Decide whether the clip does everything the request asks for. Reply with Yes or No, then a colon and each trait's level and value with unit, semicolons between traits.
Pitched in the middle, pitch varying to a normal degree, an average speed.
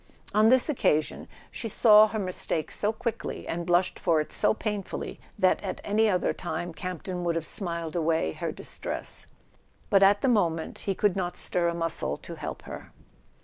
Yes: medium, 180 Hz; average, 3.9 semitones; average, 180 wpm